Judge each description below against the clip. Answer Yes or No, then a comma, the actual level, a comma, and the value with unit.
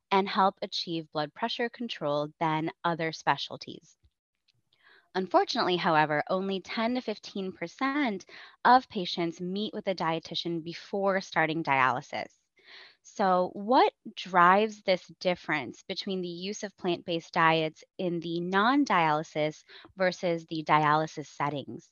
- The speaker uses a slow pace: Yes, slow, 115 wpm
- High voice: No, medium, 180 Hz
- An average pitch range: Yes, average, 3.7 semitones